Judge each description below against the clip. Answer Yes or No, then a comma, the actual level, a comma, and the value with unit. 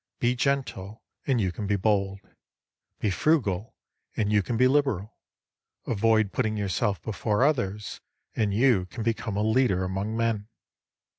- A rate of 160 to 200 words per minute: No, average, 145 wpm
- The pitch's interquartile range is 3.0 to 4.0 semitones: Yes, average, 3.3 semitones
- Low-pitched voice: Yes, low, 110 Hz